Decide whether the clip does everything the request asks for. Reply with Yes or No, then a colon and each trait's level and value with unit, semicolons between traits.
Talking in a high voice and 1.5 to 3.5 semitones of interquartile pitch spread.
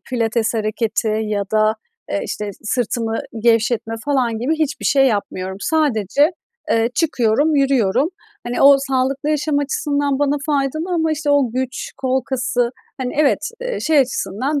No: very high, 260 Hz; average, 4.3 semitones